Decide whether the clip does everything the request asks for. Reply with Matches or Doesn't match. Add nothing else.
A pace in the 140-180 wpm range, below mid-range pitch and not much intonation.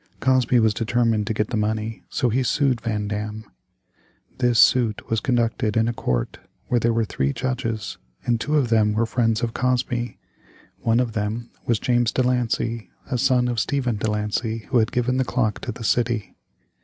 Doesn't match